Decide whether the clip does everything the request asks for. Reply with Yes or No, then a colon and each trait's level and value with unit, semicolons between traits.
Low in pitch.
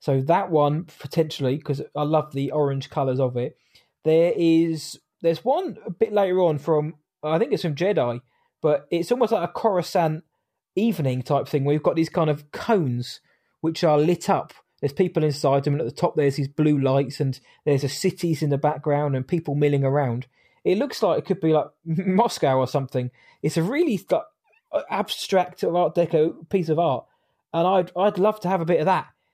No: medium, 155 Hz